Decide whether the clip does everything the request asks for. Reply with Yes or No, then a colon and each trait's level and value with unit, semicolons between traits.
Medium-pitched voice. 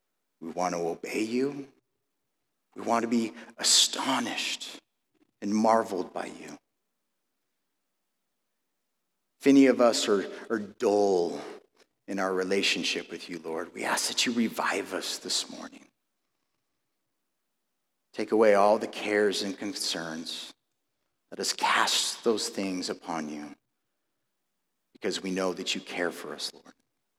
No: low, 100 Hz